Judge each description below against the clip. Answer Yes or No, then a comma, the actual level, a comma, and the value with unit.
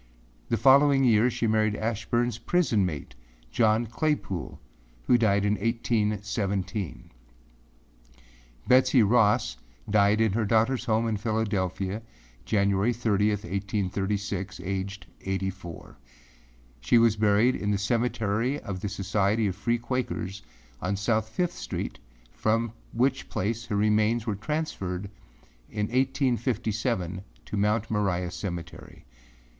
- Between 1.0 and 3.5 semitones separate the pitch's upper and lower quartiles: Yes, average, 2.8 semitones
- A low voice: Yes, low, 105 Hz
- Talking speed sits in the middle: No, slow, 120 wpm